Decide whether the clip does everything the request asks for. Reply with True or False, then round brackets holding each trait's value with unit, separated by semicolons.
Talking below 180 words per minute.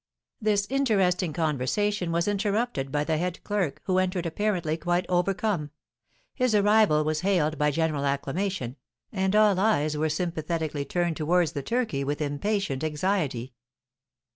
True (140 wpm)